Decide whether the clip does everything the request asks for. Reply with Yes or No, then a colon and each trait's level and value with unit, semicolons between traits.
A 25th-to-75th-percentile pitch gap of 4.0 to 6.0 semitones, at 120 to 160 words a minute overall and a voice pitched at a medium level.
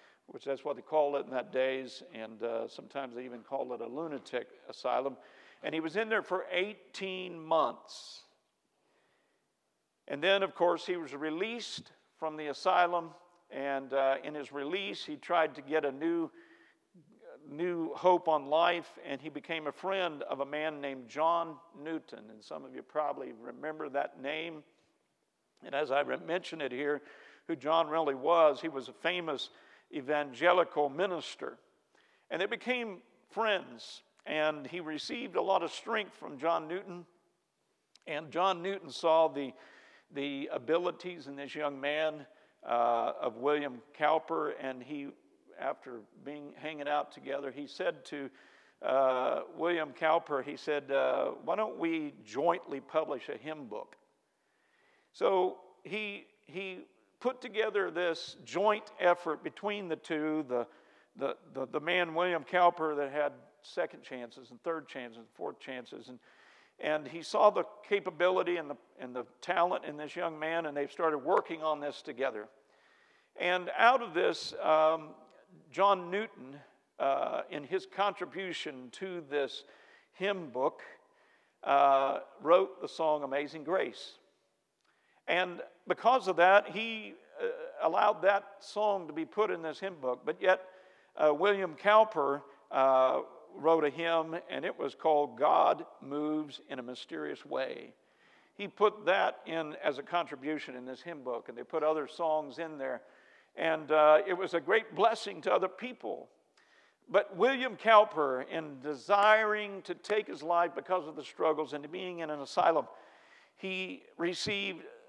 Yes: average, 4.6 semitones; average, 155 wpm; medium, 165 Hz